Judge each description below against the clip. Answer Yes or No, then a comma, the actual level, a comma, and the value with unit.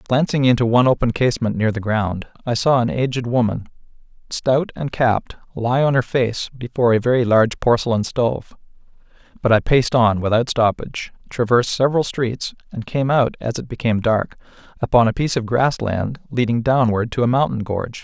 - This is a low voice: Yes, low, 120 Hz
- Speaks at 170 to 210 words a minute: Yes, average, 180 wpm